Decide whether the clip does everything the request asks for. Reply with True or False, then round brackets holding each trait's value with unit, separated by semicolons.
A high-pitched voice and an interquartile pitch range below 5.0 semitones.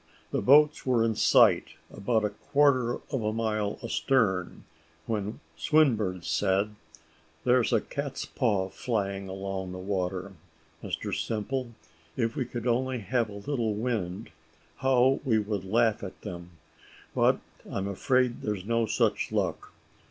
False (110 Hz; 4.2 semitones)